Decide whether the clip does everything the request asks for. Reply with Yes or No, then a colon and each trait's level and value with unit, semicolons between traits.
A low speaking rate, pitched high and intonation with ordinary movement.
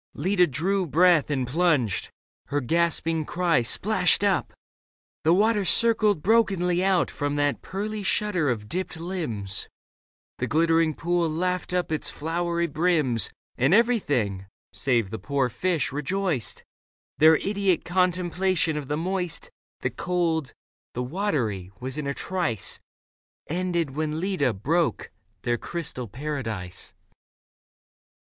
No: slow, 125 wpm; medium, 165 Hz; average, 4.8 semitones